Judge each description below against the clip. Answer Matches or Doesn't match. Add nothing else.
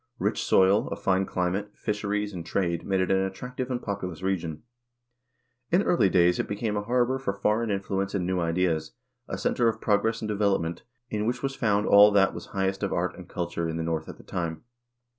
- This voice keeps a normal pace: Doesn't match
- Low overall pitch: Matches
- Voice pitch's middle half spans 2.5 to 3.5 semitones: Matches